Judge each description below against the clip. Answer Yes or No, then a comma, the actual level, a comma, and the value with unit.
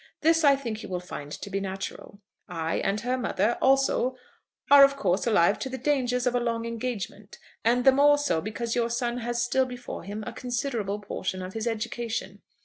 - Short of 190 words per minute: No, average, 200 wpm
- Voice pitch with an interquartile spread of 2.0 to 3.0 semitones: No, average, 4.0 semitones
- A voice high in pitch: Yes, high, 235 Hz